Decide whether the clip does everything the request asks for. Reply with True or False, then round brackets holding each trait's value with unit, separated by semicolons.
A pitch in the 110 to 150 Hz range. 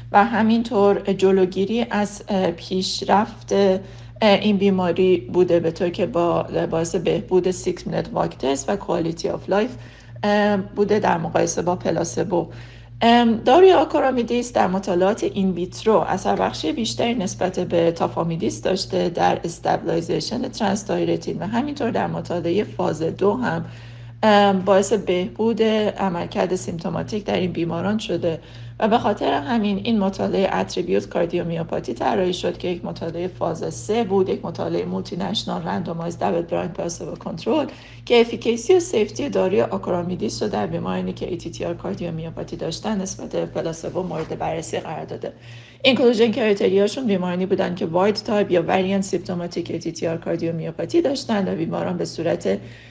False (185 Hz)